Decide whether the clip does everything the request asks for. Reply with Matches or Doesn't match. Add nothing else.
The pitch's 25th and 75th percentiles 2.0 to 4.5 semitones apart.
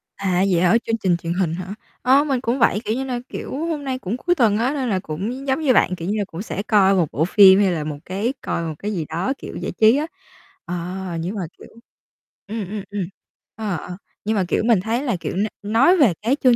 Doesn't match